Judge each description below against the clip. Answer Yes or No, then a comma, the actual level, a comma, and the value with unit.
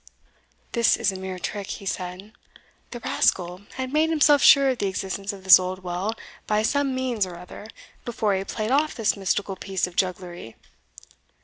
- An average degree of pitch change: Yes, average, 4.5 semitones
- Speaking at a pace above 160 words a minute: Yes, average, 180 wpm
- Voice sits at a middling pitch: No, high, 200 Hz